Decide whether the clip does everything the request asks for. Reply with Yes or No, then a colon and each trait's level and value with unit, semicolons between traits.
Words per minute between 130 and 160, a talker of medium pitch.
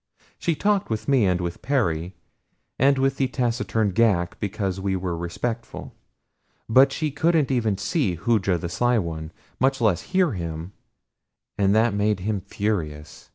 No: average, 155 wpm; low, 105 Hz